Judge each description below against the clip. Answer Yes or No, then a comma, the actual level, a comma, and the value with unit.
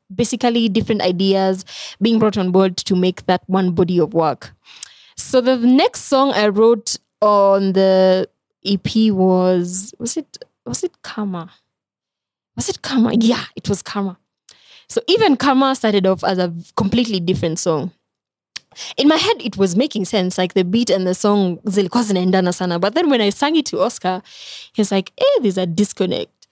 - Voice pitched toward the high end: Yes, high, 200 Hz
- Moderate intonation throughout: Yes, average, 4.1 semitones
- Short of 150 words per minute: No, average, 165 wpm